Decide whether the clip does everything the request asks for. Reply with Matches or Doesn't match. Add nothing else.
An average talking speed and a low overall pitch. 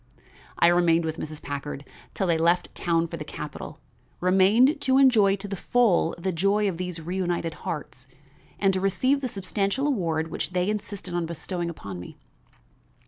Doesn't match